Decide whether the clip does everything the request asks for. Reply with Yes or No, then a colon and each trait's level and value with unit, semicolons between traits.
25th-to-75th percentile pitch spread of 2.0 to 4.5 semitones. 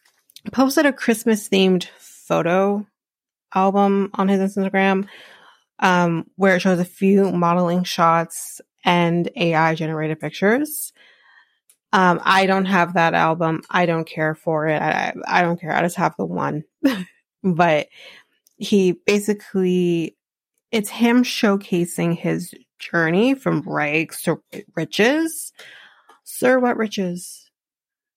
Yes: average, 3.8 semitones